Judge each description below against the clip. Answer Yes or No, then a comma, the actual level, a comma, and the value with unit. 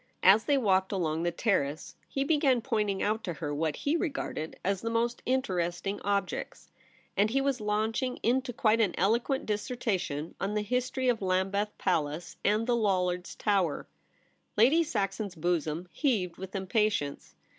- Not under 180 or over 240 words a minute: No, average, 155 wpm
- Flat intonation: No, average, 4.7 semitones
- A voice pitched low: No, high, 205 Hz